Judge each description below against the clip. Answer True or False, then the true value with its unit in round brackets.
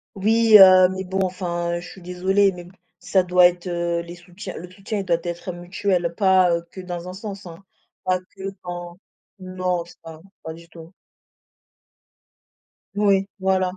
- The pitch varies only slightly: True (1.7 semitones)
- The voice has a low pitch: False (180 Hz)